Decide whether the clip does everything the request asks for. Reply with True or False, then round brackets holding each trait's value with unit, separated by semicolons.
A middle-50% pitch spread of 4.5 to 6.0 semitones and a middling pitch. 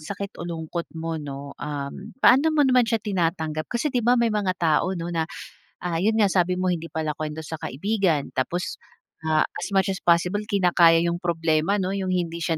False (3.7 semitones; 175 Hz)